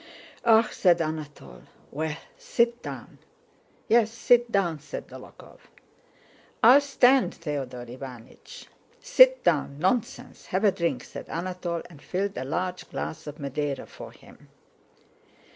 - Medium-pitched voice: Yes, medium, 175 Hz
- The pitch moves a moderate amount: No, wide, 7.8 semitones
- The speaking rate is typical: No, slow, 125 wpm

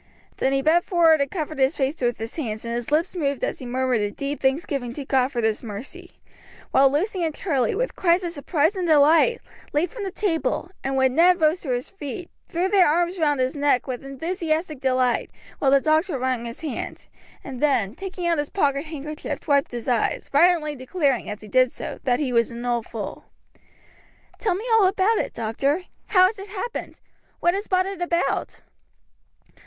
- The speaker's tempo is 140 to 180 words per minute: No, average, 200 wpm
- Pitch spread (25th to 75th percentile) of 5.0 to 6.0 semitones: Yes, average, 5.3 semitones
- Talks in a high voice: Yes, very high, 295 Hz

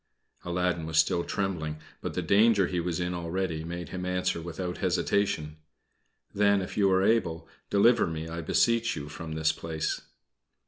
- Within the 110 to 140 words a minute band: No, average, 165 wpm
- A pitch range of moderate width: Yes, average, 3.0 semitones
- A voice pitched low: Yes, very low, 90 Hz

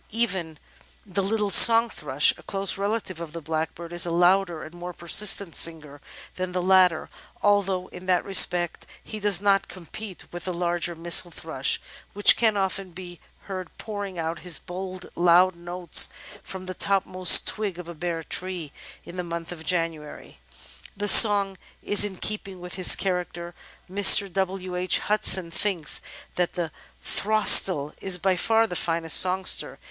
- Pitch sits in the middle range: Yes, medium, 180 Hz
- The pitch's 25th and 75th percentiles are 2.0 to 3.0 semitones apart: Yes, narrow, 2.4 semitones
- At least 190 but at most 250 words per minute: No, average, 160 wpm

